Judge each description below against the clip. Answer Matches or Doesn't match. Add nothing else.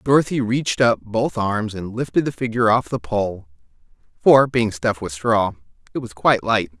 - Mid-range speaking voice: Doesn't match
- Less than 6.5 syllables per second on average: Matches